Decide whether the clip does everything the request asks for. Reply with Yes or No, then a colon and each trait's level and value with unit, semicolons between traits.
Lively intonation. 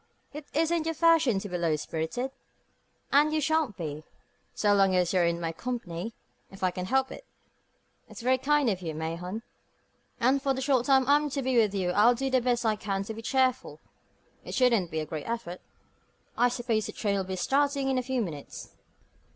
Yes: wide, 6.4 semitones